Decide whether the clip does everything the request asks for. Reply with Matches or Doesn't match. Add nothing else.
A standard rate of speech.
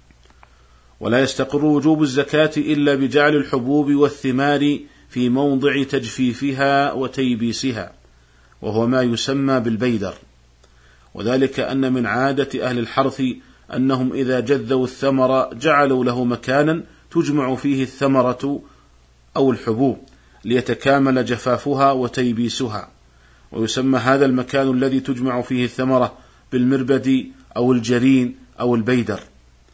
Matches